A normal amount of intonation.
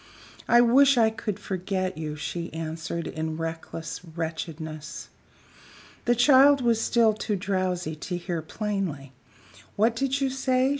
No: wide, 6.5 semitones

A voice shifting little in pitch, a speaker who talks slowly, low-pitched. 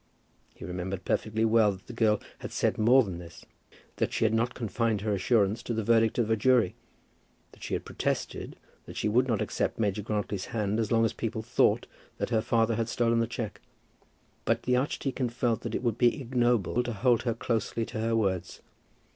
No: narrow, 2.1 semitones; fast, 205 wpm; low, 115 Hz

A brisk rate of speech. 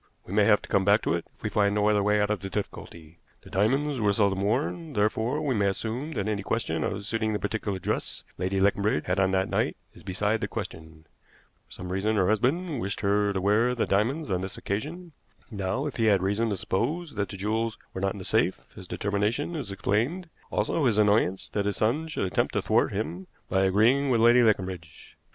Yes: fast, 225 wpm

